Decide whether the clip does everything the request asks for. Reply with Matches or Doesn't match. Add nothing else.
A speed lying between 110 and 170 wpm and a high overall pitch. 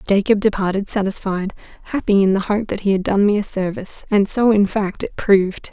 Doesn't match